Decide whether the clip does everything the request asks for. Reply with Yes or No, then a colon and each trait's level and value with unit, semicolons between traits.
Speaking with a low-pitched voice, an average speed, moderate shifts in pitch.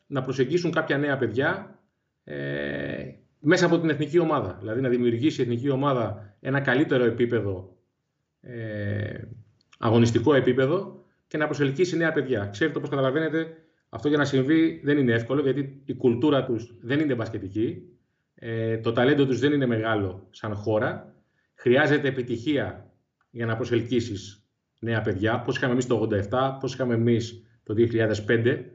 Yes: low, 125 Hz; average, 150 wpm; average, 4.3 semitones